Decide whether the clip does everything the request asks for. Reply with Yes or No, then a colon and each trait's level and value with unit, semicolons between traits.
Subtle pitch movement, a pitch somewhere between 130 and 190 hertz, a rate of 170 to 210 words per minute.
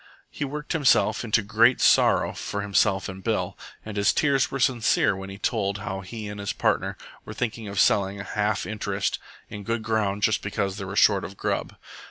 No: narrow, 2.2 semitones; low, 105 Hz; fast, 205 wpm